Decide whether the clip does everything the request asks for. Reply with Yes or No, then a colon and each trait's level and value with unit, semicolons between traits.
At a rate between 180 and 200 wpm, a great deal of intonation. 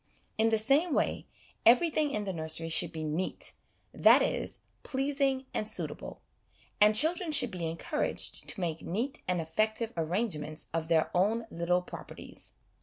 No: average, 160 wpm; wide, 8.0 semitones